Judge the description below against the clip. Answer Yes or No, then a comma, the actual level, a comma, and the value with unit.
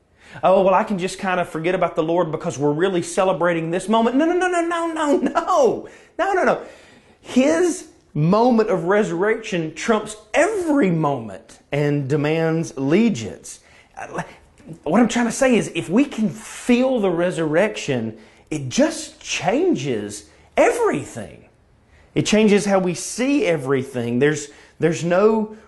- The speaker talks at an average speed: Yes, average, 145 wpm